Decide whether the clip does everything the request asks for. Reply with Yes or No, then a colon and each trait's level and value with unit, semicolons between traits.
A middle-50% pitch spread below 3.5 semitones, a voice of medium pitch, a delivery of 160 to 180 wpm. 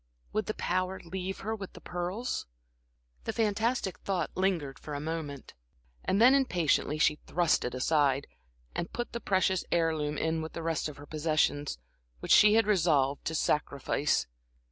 No: average, 4.4 semitones; medium, 165 Hz; average, 165 wpm